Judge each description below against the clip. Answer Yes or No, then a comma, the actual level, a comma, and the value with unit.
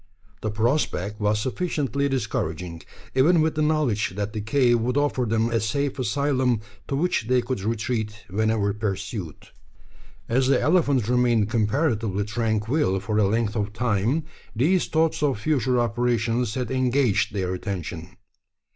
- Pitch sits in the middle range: No, low, 115 Hz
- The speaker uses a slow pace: No, average, 145 wpm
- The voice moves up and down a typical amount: Yes, average, 4.0 semitones